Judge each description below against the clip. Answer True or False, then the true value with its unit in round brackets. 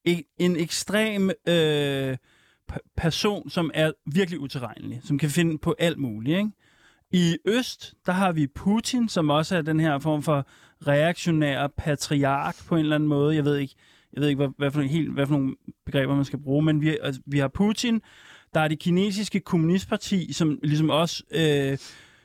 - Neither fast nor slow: True (185 wpm)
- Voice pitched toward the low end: False (155 Hz)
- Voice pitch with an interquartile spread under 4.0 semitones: True (3.6 semitones)